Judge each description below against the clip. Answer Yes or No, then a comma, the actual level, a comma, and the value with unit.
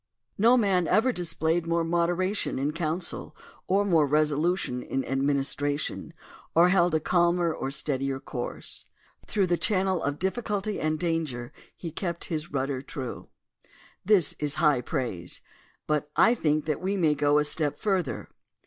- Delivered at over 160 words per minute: No, average, 150 wpm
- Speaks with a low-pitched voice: No, medium, 160 Hz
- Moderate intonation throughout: Yes, average, 3.9 semitones